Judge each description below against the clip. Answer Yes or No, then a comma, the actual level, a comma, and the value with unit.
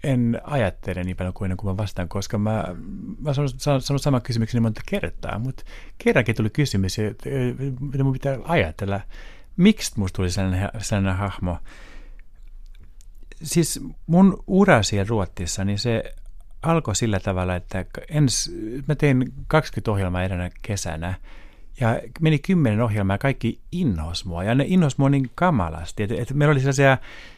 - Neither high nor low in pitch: No, low, 110 Hz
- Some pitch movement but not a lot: No, wide, 6.3 semitones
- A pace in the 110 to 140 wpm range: No, average, 150 wpm